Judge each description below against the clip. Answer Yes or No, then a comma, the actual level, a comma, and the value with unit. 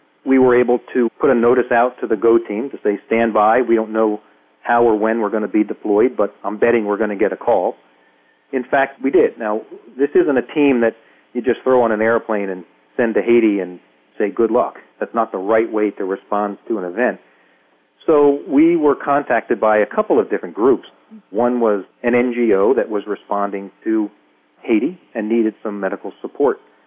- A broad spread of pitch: No, average, 3.0 semitones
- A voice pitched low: Yes, low, 110 Hz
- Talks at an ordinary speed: No, fast, 210 wpm